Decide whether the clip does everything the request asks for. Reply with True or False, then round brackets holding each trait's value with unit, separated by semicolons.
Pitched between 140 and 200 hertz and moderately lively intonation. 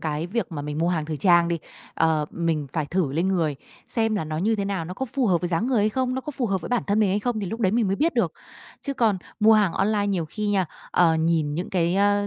True (190 Hz; 4.7 semitones)